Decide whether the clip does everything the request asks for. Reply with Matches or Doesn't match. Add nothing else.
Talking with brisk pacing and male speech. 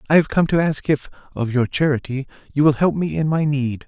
Matches